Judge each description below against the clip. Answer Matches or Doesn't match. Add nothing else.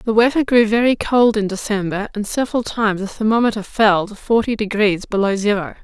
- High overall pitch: Matches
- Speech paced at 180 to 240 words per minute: Matches